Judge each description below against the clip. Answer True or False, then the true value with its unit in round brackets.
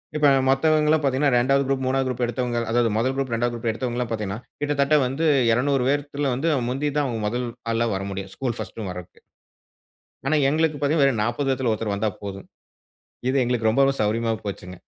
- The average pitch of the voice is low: True (125 Hz)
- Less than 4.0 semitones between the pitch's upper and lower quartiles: True (3.5 semitones)